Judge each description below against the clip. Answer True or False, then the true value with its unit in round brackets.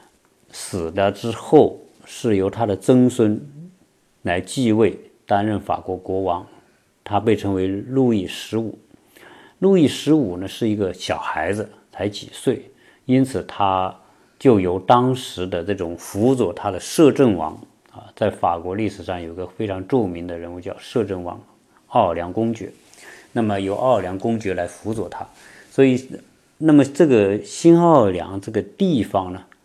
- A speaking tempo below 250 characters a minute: True (225 characters per minute)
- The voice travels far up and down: False (4.9 semitones)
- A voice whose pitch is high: False (105 Hz)